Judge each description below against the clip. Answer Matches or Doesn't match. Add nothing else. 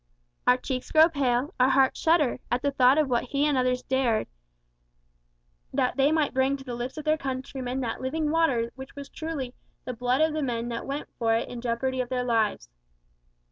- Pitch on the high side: Matches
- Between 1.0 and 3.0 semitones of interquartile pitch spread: Matches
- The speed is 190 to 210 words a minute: Matches